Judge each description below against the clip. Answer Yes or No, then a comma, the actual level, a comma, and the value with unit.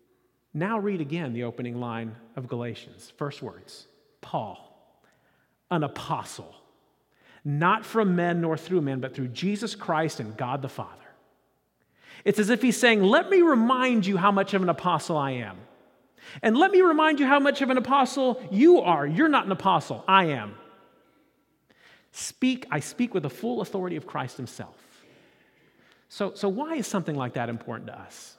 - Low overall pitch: No, medium, 180 Hz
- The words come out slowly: No, average, 170 wpm